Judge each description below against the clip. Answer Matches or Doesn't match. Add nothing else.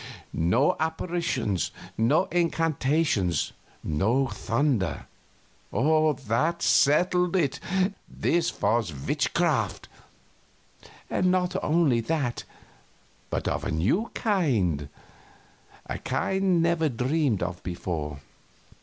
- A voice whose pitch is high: Doesn't match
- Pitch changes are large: Matches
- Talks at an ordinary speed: Doesn't match